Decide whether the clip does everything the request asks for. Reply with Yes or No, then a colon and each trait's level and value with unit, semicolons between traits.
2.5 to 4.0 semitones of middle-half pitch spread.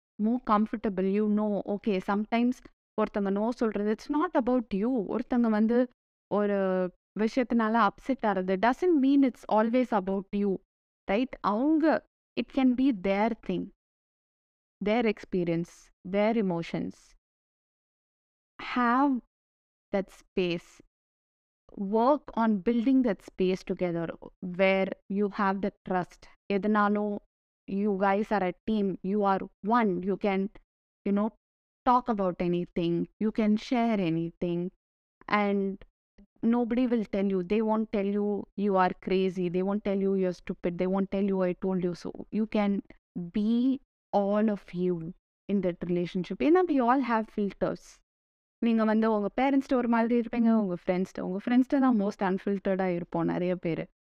Yes: average, 3.4 semitones